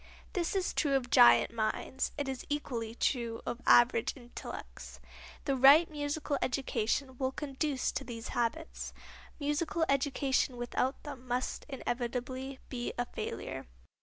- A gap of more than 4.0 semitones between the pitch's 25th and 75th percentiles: No, average, 3.0 semitones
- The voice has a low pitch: No, very high, 265 Hz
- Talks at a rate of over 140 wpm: No, slow, 135 wpm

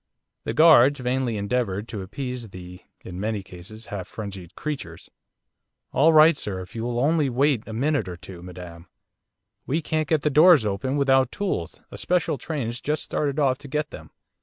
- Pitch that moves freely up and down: Yes, wide, 6.9 semitones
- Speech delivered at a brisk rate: No, average, 175 wpm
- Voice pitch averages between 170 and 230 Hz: No, low, 125 Hz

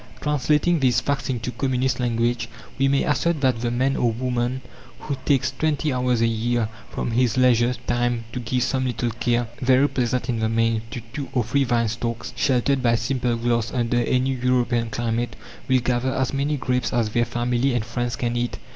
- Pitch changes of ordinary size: No, narrow, 1.8 semitones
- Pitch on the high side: No, low, 120 Hz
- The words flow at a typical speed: Yes, average, 190 wpm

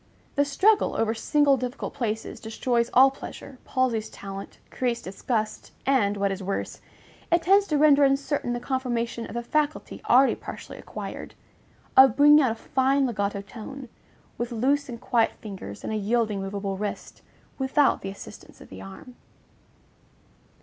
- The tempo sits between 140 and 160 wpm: Yes, average, 155 wpm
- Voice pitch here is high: Yes, high, 240 Hz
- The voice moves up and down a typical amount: Yes, average, 4.4 semitones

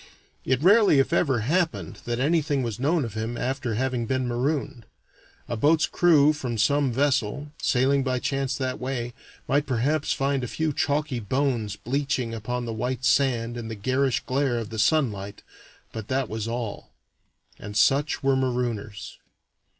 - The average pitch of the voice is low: Yes, low, 130 Hz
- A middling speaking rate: Yes, average, 160 wpm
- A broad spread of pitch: No, average, 3.3 semitones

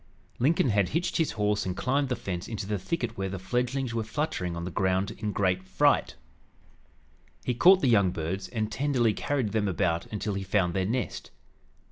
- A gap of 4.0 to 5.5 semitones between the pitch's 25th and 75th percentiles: Yes, average, 4.8 semitones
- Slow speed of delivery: No, average, 190 wpm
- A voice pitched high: No, low, 105 Hz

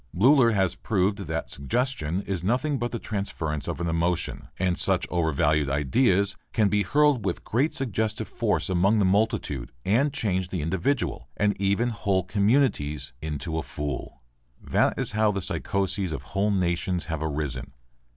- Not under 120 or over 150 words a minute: No, average, 160 wpm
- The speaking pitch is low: Yes, very low, 95 Hz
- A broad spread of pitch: No, average, 4.9 semitones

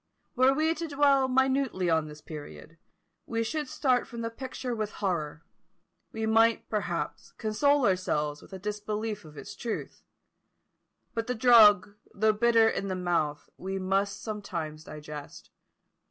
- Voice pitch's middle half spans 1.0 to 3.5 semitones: No, average, 5.3 semitones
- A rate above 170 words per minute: No, average, 145 wpm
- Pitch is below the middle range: No, high, 210 Hz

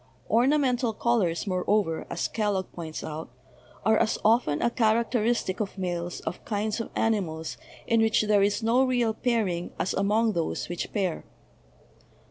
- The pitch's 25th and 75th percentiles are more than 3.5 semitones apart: Yes, average, 4.2 semitones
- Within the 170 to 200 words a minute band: No, average, 150 wpm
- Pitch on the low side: No, high, 215 Hz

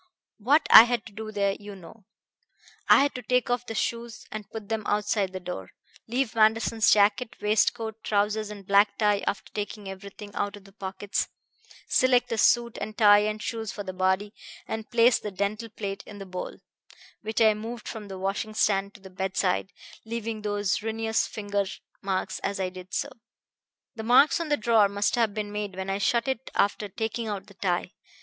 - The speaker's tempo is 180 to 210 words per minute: Yes, average, 195 wpm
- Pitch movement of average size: No, narrow, 2.1 semitones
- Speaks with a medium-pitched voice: No, high, 210 Hz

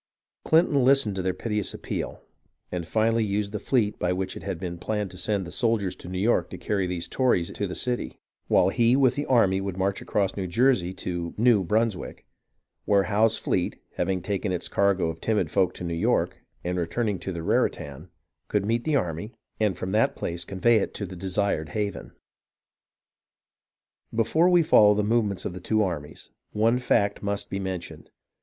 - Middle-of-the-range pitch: No, low, 100 Hz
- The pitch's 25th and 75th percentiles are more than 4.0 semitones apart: No, average, 3.6 semitones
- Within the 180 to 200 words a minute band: Yes, average, 190 wpm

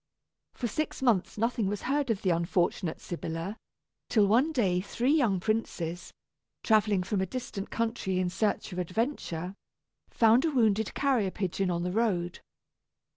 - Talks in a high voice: Yes, high, 205 Hz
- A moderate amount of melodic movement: Yes, average, 4.4 semitones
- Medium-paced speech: Yes, average, 150 wpm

